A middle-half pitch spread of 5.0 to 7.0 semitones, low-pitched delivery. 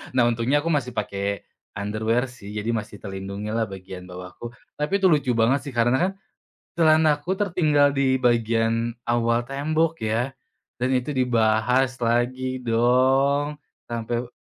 No: average, 3.6 semitones; low, 120 Hz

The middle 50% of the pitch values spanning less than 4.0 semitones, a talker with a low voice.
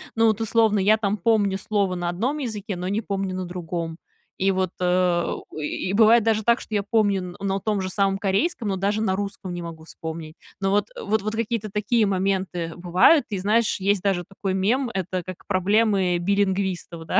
No: average, 2.7 semitones; high, 195 Hz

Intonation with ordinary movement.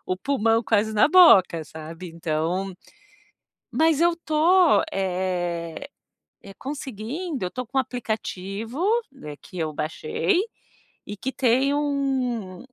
No: wide, 7.5 semitones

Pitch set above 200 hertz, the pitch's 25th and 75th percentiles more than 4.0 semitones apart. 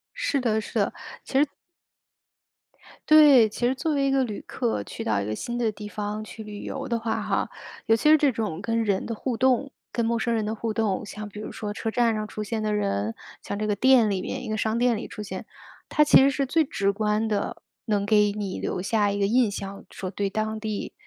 No: high, 220 Hz; average, 2.8 semitones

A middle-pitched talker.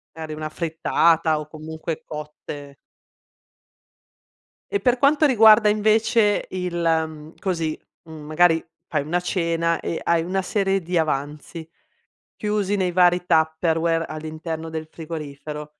Yes: medium, 165 Hz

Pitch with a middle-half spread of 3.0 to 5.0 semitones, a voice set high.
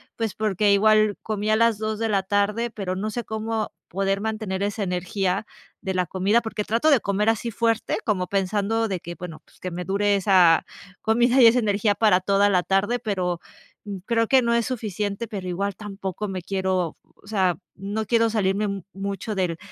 No: narrow, 2.5 semitones; high, 205 Hz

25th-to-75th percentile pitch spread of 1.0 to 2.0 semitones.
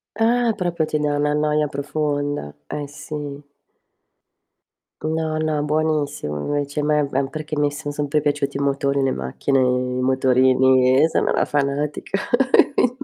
Yes: narrow, 1.7 semitones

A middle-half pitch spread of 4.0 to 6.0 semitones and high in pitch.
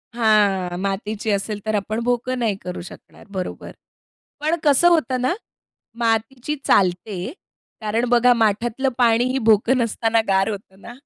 No: average, 3.5 semitones; high, 225 Hz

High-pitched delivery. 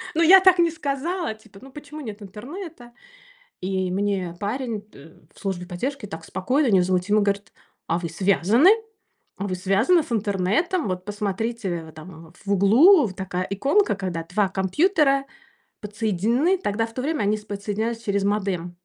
Yes: high, 205 Hz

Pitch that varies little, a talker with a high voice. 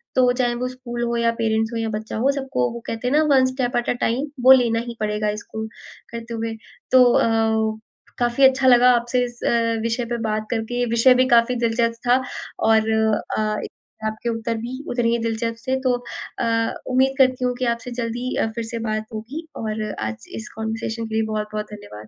Yes: narrow, 2.2 semitones; high, 230 Hz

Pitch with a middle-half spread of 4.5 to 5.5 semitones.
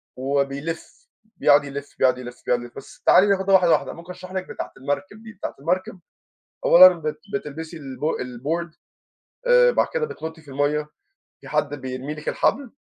Yes: average, 4.8 semitones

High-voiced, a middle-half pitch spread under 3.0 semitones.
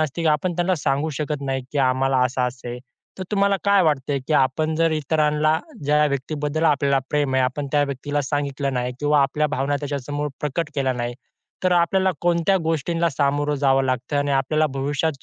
No: medium, 145 Hz; narrow, 2.6 semitones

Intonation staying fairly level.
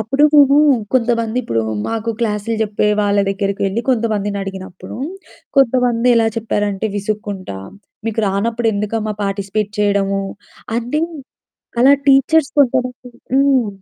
No: average, 3.4 semitones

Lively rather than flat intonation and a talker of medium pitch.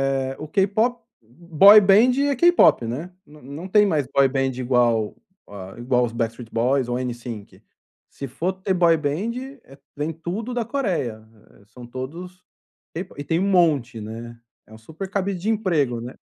Yes: wide, 7.7 semitones; medium, 150 Hz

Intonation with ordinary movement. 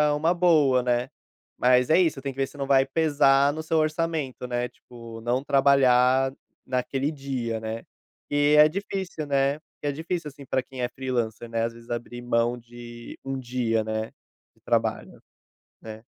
Yes: average, 3.3 semitones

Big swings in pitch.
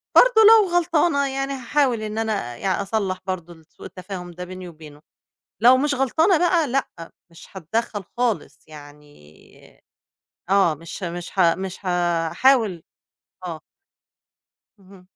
Yes: wide, 7.8 semitones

